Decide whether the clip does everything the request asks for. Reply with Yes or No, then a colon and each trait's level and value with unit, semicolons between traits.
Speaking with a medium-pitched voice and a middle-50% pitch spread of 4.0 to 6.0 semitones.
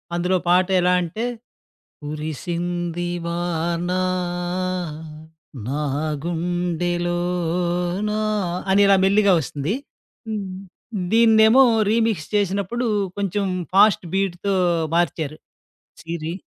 No: medium, 175 Hz; average, 2.7 semitones